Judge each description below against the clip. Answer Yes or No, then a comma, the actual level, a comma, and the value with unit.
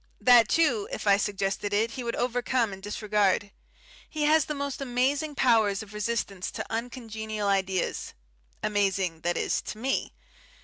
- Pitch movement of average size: Yes, average, 3.7 semitones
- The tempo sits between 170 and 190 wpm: No, average, 150 wpm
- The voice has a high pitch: Yes, high, 220 Hz